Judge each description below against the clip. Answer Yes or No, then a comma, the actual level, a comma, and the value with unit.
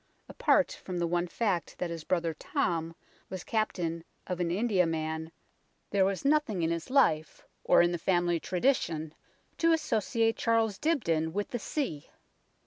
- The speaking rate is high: No, average, 150 wpm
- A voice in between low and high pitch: Yes, medium, 180 Hz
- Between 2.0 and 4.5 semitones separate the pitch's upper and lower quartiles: No, average, 5.1 semitones